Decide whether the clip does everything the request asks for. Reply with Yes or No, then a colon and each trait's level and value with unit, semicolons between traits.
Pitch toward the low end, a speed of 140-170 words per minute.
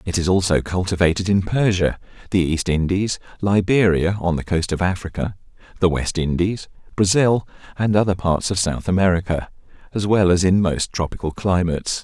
Yes: very low, 90 Hz; average, 160 wpm